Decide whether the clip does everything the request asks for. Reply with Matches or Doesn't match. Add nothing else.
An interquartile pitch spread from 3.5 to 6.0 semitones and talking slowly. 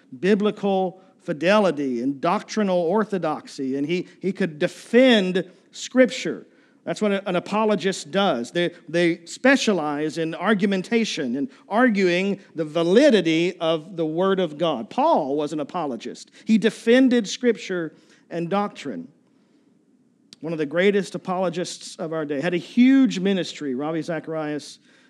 Matches